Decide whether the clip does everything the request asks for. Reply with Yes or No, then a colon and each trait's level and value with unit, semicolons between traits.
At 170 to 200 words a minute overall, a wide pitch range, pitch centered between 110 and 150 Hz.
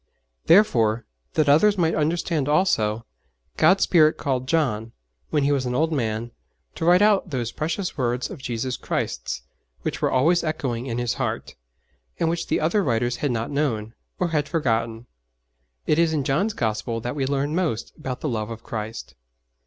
Yes: average, 175 wpm; wide, 5.7 semitones; low, 135 Hz